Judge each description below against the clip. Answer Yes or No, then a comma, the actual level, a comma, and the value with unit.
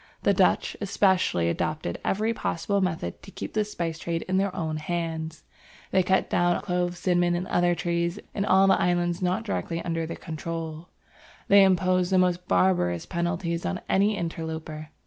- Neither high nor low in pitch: Yes, medium, 175 Hz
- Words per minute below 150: No, average, 170 wpm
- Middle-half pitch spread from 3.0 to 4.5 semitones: No, narrow, 2.4 semitones